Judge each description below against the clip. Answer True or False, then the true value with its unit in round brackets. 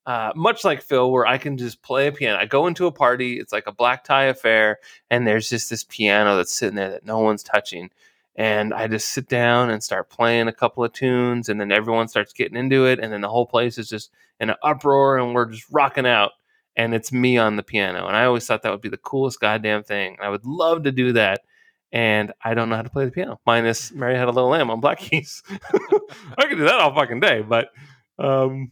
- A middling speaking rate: False (245 wpm)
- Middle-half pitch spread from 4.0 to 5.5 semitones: False (3.4 semitones)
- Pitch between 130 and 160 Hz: False (120 Hz)